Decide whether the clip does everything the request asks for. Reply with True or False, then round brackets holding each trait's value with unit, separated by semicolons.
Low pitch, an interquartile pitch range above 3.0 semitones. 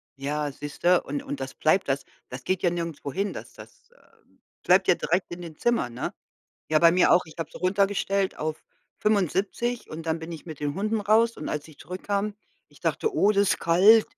False (175 Hz; 4.5 semitones)